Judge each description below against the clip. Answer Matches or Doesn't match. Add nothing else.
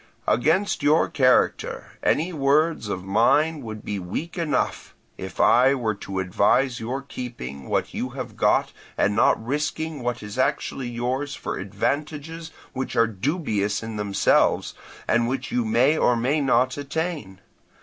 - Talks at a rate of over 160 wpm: Doesn't match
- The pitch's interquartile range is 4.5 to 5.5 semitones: Matches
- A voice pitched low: Matches